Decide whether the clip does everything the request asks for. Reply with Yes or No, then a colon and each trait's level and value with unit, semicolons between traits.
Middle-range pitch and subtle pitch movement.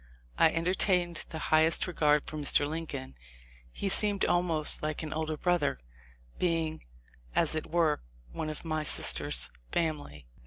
Yes: medium, 160 Hz; narrow, 2.1 semitones